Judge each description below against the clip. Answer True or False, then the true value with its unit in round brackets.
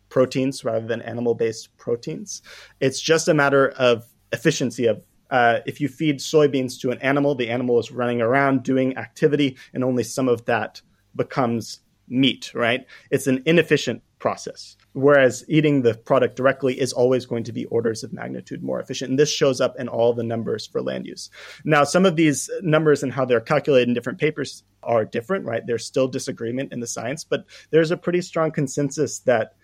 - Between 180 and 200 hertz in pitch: False (130 Hz)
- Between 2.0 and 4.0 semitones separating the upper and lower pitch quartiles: True (3.5 semitones)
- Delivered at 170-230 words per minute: True (190 wpm)